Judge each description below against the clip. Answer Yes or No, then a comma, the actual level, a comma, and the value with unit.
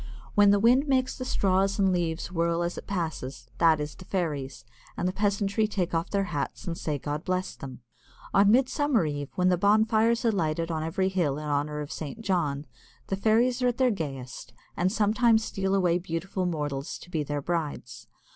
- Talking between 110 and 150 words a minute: No, average, 195 wpm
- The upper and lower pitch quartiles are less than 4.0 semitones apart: No, average, 4.9 semitones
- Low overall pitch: No, medium, 180 Hz